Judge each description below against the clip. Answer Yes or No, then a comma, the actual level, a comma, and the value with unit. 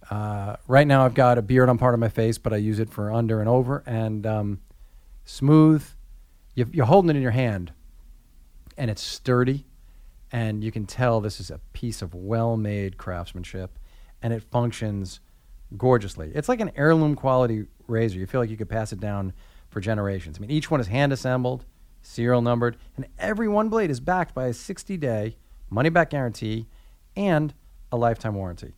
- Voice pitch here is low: Yes, low, 115 Hz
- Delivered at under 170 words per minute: No, average, 190 wpm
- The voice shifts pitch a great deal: No, average, 4.5 semitones